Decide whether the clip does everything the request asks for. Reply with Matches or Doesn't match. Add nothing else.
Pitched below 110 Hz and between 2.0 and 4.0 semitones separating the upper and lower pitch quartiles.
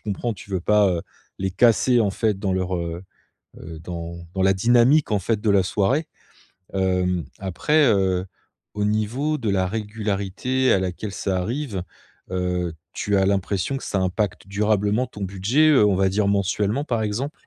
Matches